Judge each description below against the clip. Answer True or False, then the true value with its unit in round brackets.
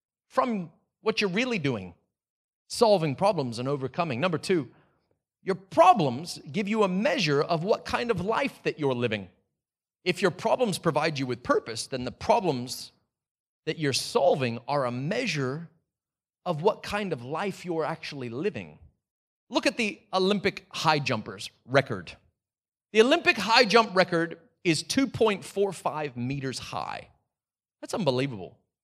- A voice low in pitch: False (155 Hz)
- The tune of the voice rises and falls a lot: True (8.0 semitones)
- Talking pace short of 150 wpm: True (140 wpm)